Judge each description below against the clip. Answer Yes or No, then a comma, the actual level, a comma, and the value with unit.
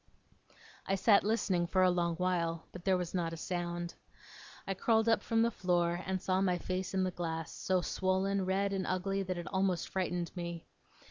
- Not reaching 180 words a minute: No, average, 195 wpm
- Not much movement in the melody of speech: Yes, narrow, 1.8 semitones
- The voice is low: No, medium, 185 Hz